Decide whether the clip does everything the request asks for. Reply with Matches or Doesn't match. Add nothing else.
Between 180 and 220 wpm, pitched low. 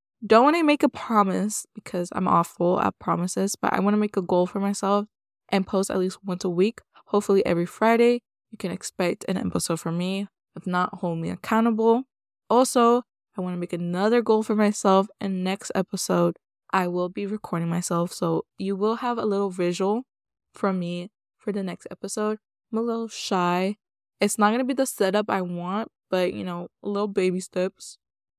Doesn't match